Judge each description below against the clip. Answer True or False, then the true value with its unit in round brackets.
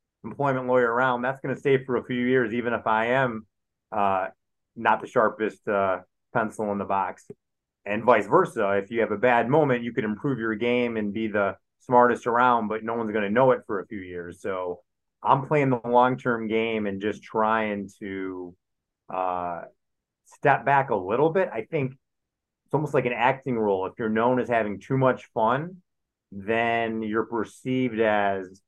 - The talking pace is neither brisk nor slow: True (190 wpm)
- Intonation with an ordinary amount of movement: True (3.4 semitones)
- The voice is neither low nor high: False (115 Hz)